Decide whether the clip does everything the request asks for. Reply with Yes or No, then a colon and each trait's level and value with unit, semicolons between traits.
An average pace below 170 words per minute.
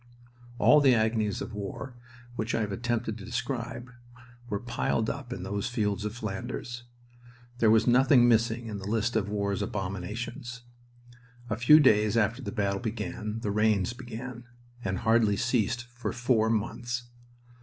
Yes: average, 155 wpm